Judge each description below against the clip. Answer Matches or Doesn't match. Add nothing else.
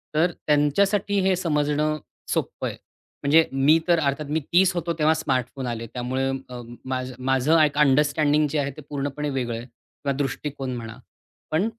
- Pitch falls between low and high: Matches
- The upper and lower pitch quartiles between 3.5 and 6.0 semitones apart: Doesn't match